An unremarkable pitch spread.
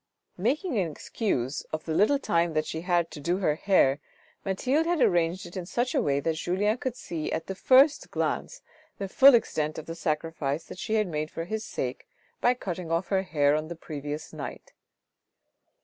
No: wide, 5.7 semitones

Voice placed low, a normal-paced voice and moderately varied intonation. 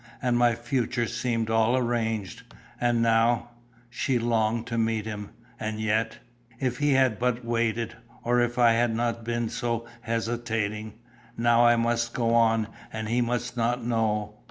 No: low, 115 Hz; average, 160 wpm; narrow, 1.2 semitones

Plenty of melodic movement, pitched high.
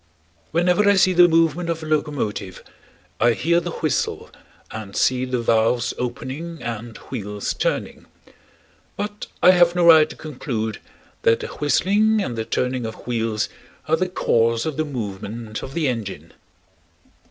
No: wide, 6.8 semitones; low, 130 Hz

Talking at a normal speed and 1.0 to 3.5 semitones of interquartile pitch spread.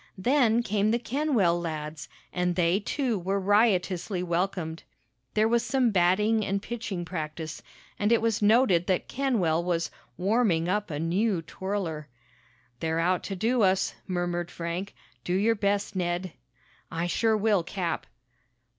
No: average, 145 wpm; average, 4.0 semitones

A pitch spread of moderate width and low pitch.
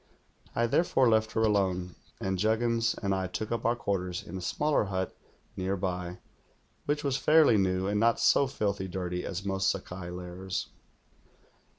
Yes: average, 3.8 semitones; low, 100 Hz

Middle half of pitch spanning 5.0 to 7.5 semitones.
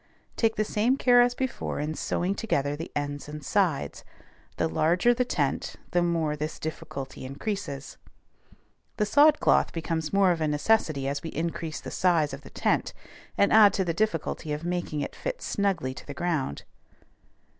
Yes: wide, 5.6 semitones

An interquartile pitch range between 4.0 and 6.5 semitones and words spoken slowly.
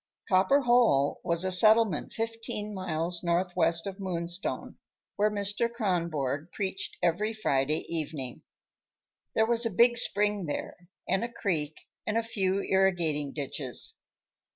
Yes: average, 4.5 semitones; slow, 130 wpm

